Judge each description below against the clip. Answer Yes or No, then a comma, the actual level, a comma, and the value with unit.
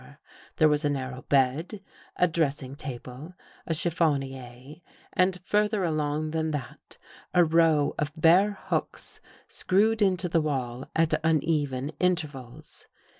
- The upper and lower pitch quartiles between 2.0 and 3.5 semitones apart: No, average, 4.0 semitones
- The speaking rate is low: Yes, slow, 125 wpm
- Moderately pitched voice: Yes, medium, 155 Hz